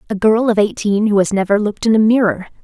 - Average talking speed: No, fast, 250 wpm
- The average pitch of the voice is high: Yes, high, 210 Hz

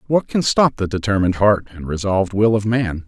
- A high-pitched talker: No, low, 105 Hz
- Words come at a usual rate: No, fast, 215 wpm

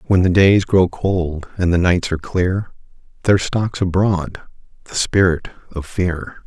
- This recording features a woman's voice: No, male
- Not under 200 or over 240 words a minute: No, average, 160 wpm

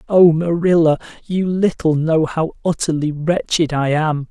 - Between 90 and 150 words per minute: Yes, average, 140 wpm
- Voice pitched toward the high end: No, medium, 160 Hz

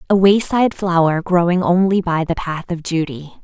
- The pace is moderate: Yes, average, 175 wpm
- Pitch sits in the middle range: Yes, medium, 180 Hz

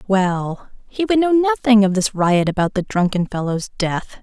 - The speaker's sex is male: No, female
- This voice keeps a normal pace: Yes, average, 185 wpm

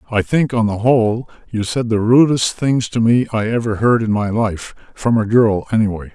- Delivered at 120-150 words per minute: No, fast, 205 wpm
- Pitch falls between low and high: No, low, 110 Hz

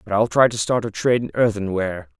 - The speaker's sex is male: Yes, male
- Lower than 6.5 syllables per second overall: No, 7.1 syllables/s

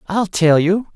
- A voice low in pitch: No, medium, 185 Hz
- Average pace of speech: Yes, average, 190 wpm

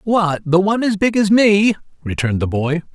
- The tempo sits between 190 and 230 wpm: Yes, fast, 205 wpm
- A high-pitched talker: No, medium, 180 Hz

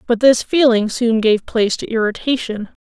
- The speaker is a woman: Yes, female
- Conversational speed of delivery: Yes, average, 170 wpm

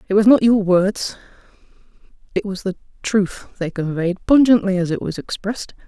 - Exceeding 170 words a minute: No, average, 165 wpm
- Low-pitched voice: No, high, 200 Hz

